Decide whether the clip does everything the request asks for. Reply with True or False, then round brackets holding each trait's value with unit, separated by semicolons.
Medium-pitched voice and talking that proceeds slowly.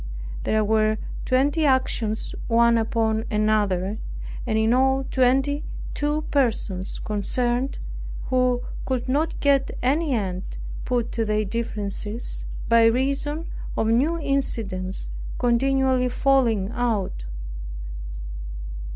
False (240 Hz; 100 wpm)